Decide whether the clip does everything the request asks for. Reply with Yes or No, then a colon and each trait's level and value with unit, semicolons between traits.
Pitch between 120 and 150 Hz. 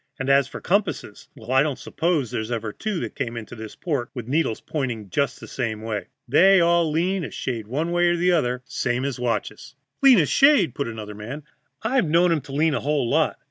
Yes: medium, 140 Hz